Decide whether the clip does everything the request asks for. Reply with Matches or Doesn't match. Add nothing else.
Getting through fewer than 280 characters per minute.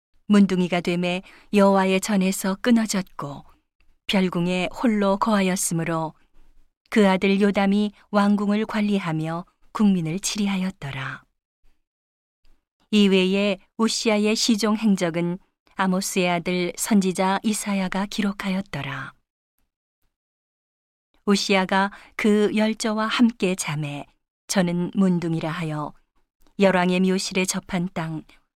Matches